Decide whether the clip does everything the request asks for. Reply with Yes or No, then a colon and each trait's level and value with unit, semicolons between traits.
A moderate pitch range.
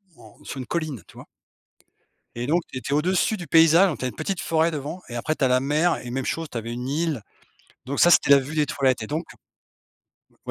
Yes: average, 4.3 semitones